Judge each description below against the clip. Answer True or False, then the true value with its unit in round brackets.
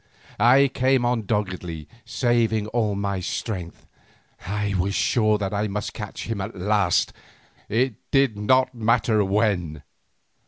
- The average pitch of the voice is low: True (105 Hz)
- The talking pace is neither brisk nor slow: False (125 wpm)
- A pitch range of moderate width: True (3.2 semitones)